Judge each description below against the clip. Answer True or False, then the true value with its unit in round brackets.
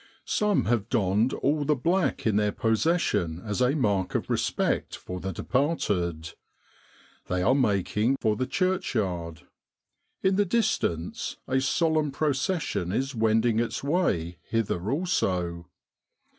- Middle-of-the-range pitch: False (115 Hz)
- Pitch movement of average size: False (8.2 semitones)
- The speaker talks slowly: True (130 wpm)